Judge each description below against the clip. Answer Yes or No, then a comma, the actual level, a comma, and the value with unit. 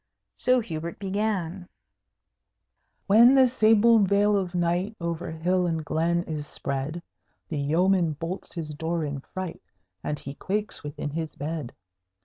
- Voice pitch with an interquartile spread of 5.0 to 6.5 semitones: No, average, 4.0 semitones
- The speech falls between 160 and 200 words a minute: No, slow, 135 wpm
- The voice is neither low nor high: Yes, medium, 170 Hz